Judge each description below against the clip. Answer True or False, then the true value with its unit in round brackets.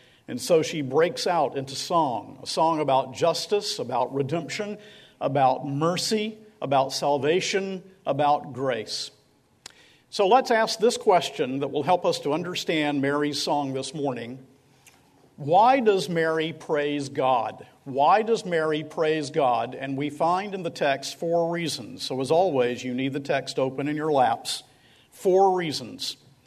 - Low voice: False (150 Hz)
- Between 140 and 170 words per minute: True (145 wpm)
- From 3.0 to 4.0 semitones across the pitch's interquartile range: False (5.0 semitones)